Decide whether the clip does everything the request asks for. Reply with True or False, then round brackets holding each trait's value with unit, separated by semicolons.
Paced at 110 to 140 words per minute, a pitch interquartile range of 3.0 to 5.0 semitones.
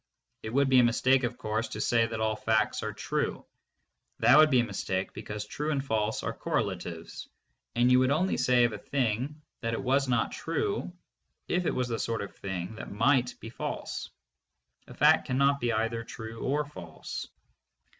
False (185 wpm; 3.6 semitones)